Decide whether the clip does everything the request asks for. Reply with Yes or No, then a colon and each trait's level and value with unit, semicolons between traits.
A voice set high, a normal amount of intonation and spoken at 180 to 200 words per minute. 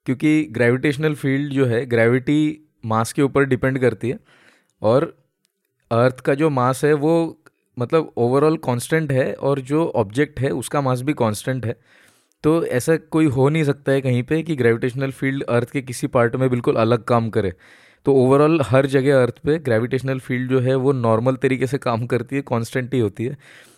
No: low, 135 Hz; average, 3.3 semitones; average, 185 wpm